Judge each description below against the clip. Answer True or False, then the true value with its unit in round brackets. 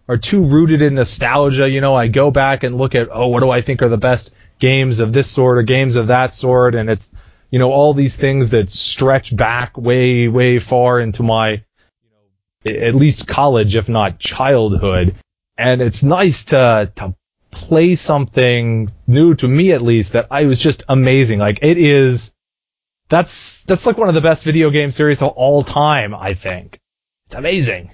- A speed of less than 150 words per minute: False (195 wpm)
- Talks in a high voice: False (125 Hz)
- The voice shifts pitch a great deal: False (3.8 semitones)